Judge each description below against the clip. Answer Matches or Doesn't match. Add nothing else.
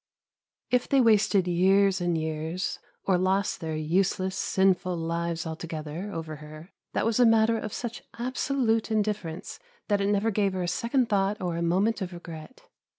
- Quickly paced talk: Doesn't match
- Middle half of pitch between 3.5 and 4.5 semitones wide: Matches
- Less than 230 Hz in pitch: Matches